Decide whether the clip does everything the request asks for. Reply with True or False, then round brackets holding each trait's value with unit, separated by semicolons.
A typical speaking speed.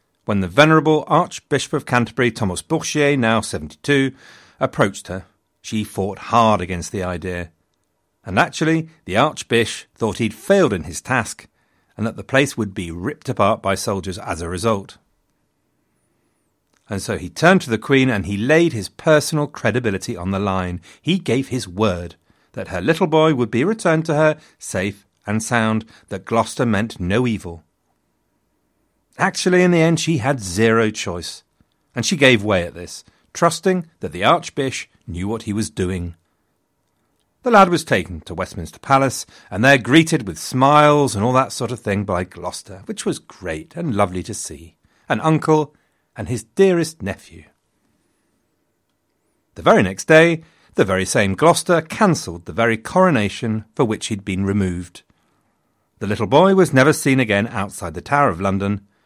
True (165 wpm)